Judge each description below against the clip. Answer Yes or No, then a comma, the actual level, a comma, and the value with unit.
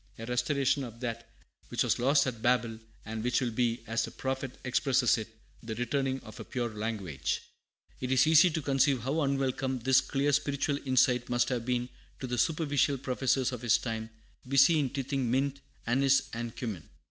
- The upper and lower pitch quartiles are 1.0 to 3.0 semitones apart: Yes, narrow, 2.6 semitones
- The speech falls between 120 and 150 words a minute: No, average, 180 wpm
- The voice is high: No, low, 125 Hz